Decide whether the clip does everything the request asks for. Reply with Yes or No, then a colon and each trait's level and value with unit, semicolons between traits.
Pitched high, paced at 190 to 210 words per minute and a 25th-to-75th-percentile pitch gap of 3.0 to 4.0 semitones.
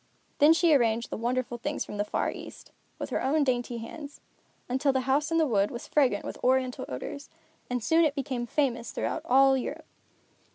Yes: very high, 260 Hz; average, 195 wpm; average, 3.3 semitones